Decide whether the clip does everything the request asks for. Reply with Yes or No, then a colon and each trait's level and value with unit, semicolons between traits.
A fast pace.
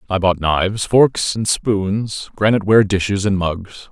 No: average, 170 wpm